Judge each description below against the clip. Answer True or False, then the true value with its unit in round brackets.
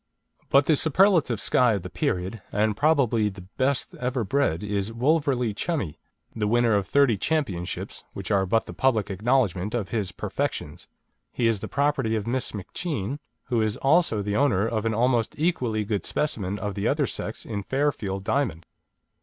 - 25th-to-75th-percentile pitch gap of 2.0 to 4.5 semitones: False (5.1 semitones)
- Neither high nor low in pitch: False (115 Hz)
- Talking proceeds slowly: False (170 wpm)